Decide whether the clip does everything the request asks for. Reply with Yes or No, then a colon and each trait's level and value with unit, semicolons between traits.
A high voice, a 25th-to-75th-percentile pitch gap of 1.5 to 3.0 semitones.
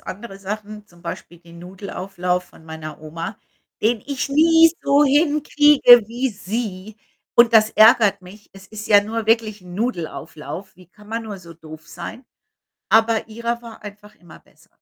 No: high, 210 Hz; average, 4.4 semitones